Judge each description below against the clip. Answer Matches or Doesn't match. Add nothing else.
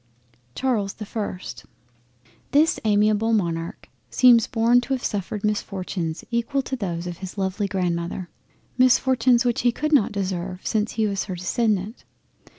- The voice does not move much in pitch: Doesn't match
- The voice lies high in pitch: Matches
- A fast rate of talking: Doesn't match